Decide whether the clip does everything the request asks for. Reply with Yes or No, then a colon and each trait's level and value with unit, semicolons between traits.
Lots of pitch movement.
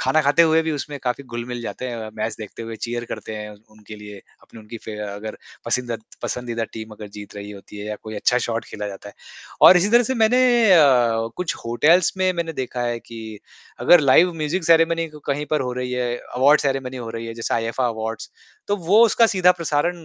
Yes: wide, 6.2 semitones